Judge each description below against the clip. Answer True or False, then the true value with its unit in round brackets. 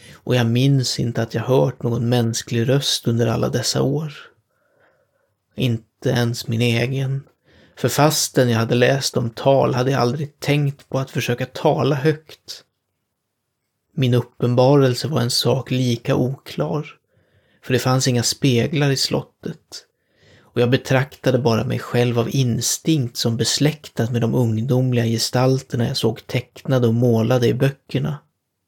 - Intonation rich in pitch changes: False (2.4 semitones)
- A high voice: False (125 Hz)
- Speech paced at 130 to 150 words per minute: True (145 wpm)